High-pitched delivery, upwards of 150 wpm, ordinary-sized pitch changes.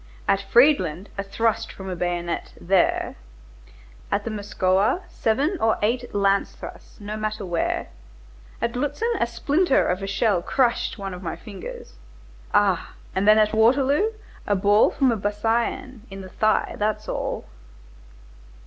No: high, 210 Hz; average, 145 wpm; average, 3.6 semitones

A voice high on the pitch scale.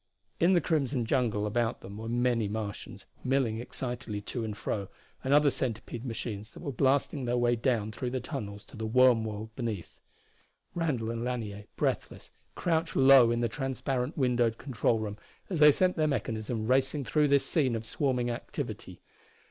No: low, 120 Hz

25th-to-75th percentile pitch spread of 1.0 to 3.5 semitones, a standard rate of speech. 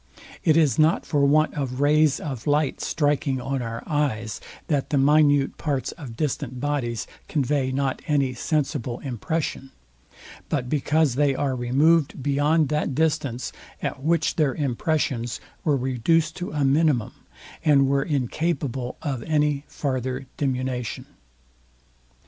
No: average, 2.7 semitones; slow, 130 wpm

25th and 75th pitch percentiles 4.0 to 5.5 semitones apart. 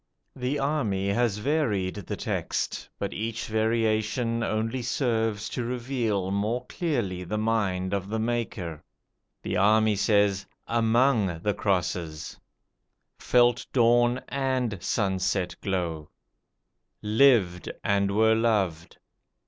No: average, 3.6 semitones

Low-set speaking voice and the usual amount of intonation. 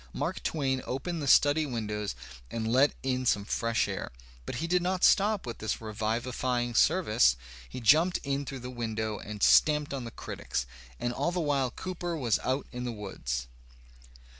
Yes: low, 125 Hz; average, 4.9 semitones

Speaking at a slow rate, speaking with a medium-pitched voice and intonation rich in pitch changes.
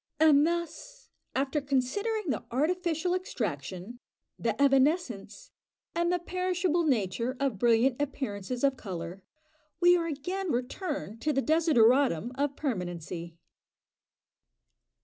No: slow, 110 wpm; very high, 275 Hz; wide, 6.7 semitones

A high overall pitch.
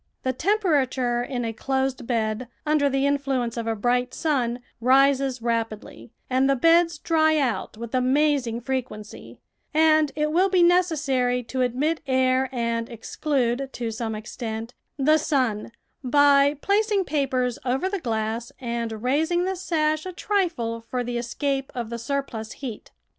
Yes: very high, 260 Hz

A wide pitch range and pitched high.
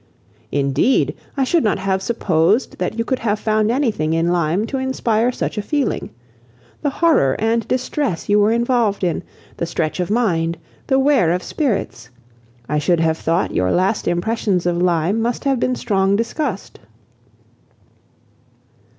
Yes: wide, 5.7 semitones; high, 205 Hz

